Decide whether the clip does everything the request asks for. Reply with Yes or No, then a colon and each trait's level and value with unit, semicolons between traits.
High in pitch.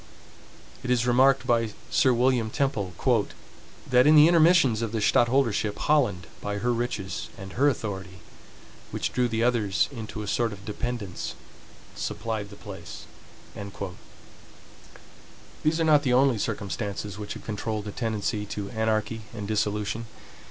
No: low, 110 Hz